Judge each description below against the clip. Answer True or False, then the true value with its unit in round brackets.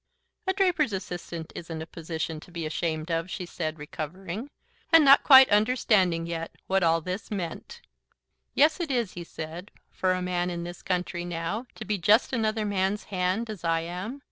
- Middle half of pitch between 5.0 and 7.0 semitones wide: False (4.6 semitones)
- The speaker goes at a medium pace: True (180 wpm)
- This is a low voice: False (180 Hz)